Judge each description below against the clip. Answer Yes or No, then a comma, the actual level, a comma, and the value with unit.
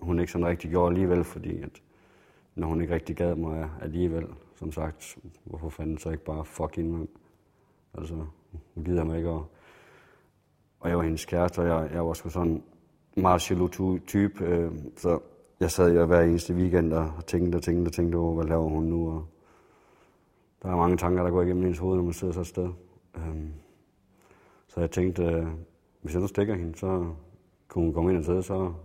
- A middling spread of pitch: No, narrow, 1.6 semitones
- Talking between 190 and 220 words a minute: Yes, average, 200 wpm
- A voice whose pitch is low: Yes, very low, 85 Hz